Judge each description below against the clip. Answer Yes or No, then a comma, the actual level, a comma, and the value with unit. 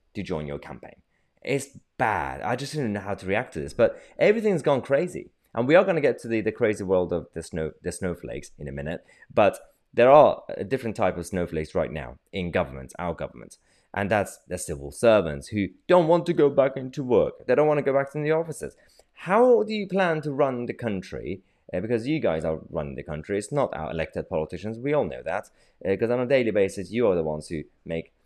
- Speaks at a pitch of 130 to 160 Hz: No, low, 105 Hz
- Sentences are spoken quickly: Yes, fast, 235 wpm